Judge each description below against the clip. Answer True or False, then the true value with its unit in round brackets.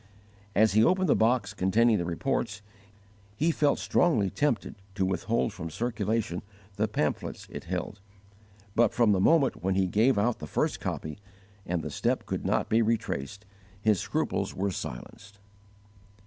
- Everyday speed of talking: True (155 wpm)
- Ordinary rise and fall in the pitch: True (3.8 semitones)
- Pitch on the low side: True (105 Hz)